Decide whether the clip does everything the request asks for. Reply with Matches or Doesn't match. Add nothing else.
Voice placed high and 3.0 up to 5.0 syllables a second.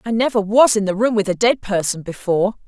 Doesn't match